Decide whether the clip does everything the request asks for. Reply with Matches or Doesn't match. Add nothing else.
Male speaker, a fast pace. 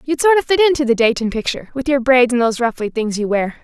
Doesn't match